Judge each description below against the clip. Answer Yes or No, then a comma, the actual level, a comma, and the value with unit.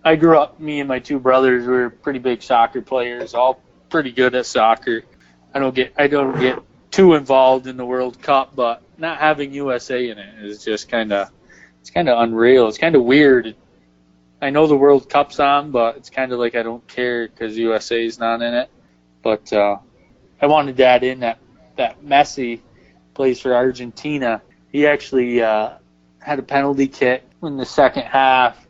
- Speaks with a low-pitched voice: Yes, low, 125 Hz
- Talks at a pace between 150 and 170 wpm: No, average, 190 wpm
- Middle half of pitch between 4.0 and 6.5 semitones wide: No, average, 3.3 semitones